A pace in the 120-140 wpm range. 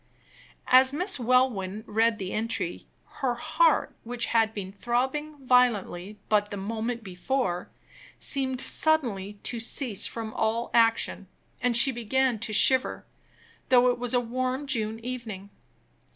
Yes: slow, 135 wpm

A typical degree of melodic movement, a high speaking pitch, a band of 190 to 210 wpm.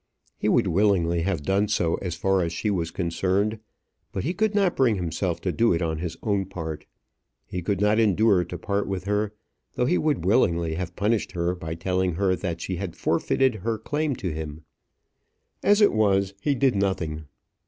No: average, 4.0 semitones; very low, 95 Hz; average, 195 wpm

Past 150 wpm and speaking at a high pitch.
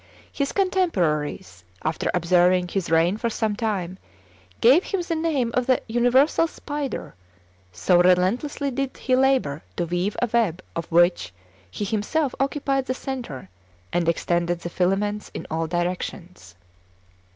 No: average, 140 wpm; high, 200 Hz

